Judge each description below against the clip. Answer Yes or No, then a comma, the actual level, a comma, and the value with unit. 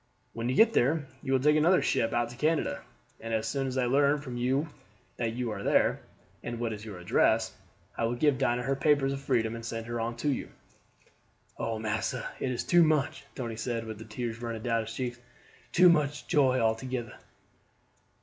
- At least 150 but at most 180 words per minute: No, fast, 205 wpm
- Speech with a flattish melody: No, average, 3.3 semitones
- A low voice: Yes, low, 120 Hz